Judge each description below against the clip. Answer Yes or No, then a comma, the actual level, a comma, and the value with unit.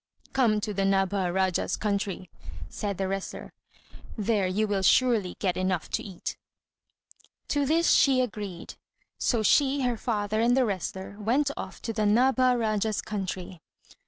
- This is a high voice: Yes, high, 210 Hz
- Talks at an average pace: Yes, average, 150 wpm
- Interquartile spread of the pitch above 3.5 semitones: Yes, average, 4.0 semitones